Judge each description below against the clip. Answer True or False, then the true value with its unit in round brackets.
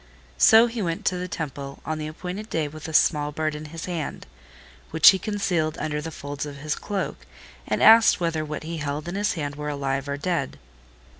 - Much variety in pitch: False (3.3 semitones)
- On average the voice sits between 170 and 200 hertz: False (155 Hz)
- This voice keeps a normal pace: False (210 wpm)